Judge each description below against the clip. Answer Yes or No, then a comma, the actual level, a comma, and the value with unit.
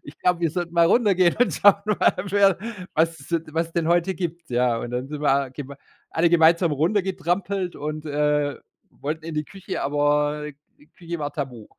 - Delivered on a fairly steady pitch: No, average, 3.1 semitones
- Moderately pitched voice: Yes, medium, 160 Hz